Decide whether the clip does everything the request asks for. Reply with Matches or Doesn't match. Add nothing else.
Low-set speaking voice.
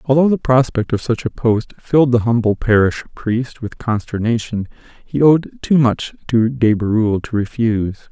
Matches